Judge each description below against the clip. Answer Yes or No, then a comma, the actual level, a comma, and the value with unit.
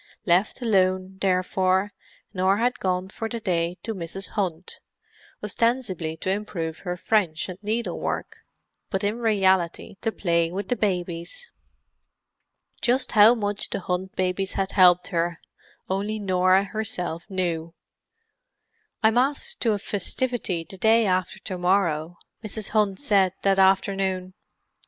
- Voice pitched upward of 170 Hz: Yes, high, 190 Hz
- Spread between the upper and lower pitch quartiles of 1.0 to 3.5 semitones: Yes, average, 2.8 semitones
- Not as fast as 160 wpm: Yes, slow, 135 wpm